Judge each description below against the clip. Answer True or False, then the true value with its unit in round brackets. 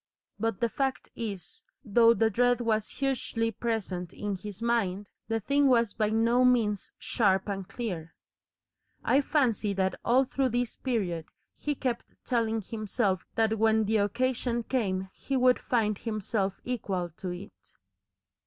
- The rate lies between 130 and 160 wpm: True (145 wpm)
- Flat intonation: False (3.5 semitones)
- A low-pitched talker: False (225 Hz)